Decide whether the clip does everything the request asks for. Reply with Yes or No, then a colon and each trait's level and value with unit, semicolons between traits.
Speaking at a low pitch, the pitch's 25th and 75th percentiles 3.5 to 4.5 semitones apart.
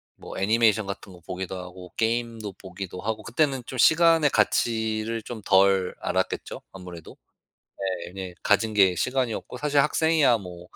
Yes: low, 110 Hz; average, 4.2 semitones